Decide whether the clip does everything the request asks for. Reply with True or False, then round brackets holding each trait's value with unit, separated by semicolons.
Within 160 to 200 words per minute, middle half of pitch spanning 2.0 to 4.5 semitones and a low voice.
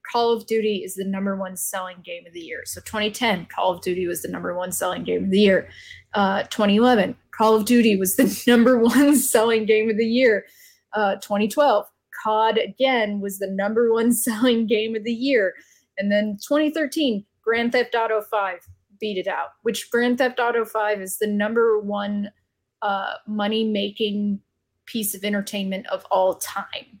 False (180 wpm; 2.9 semitones; 215 Hz)